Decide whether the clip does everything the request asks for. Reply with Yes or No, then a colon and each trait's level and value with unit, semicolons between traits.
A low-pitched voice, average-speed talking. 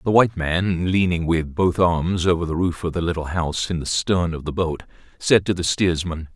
No: very low, 85 Hz; fast, 225 wpm